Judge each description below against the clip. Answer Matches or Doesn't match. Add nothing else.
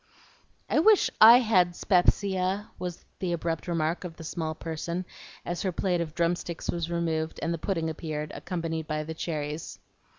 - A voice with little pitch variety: Matches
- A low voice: Doesn't match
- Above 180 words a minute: Doesn't match